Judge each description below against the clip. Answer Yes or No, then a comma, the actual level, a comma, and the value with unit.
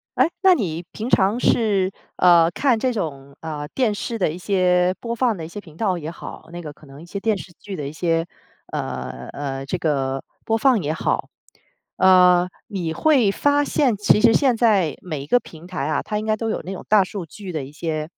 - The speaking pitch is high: No, medium, 180 Hz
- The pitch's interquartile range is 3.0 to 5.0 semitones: No, wide, 5.6 semitones